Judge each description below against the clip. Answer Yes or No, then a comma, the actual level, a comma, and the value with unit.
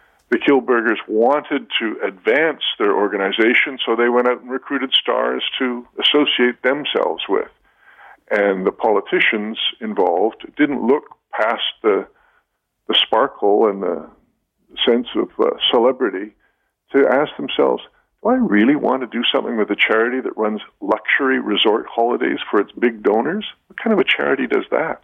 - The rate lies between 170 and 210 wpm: No, average, 150 wpm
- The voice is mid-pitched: No, low, 130 Hz